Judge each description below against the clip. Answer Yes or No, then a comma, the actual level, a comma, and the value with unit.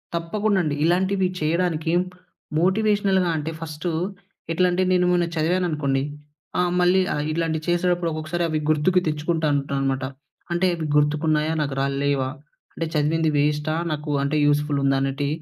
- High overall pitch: No, medium, 155 Hz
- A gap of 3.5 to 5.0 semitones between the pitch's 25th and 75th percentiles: No, average, 3.1 semitones